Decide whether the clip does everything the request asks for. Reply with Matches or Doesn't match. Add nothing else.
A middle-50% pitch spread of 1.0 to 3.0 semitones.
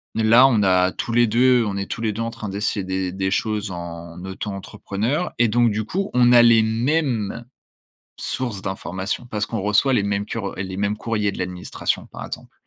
Doesn't match